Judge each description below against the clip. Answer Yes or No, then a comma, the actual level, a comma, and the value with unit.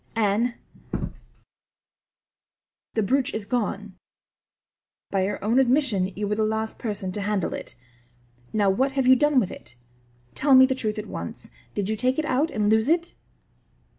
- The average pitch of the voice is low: No, high, 220 Hz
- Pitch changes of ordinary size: Yes, average, 4.1 semitones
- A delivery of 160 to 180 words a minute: Yes, average, 165 wpm